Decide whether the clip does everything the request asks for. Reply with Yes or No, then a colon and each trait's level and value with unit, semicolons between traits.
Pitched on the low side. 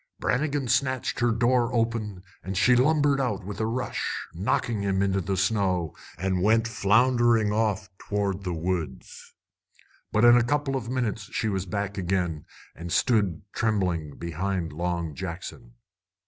Yes: low, 105 Hz